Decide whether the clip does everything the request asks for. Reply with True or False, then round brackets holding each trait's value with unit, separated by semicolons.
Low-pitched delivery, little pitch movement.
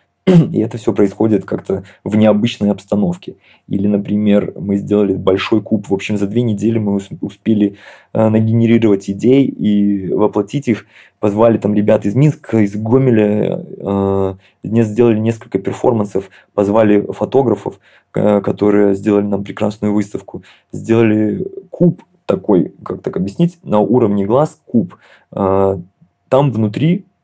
True (105 Hz; 2.3 semitones)